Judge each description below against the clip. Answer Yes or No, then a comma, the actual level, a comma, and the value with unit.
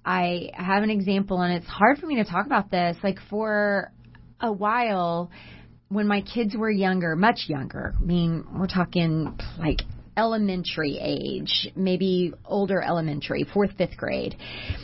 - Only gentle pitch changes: No, average, 3.0 semitones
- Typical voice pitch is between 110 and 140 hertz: No, high, 190 Hz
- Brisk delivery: No, average, 150 wpm